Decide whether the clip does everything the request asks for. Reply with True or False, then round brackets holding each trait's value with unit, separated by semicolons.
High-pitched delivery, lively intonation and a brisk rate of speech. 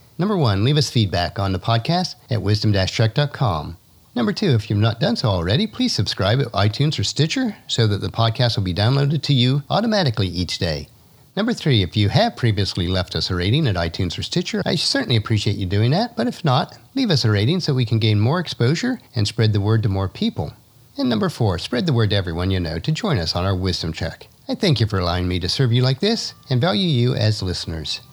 False (115 Hz; 7.2 semitones; 235 wpm)